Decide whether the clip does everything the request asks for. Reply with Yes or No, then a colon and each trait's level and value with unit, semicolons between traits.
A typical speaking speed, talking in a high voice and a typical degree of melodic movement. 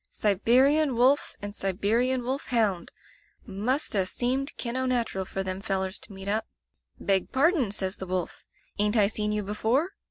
Yes: average, 180 wpm; high, 215 Hz; average, 4.7 semitones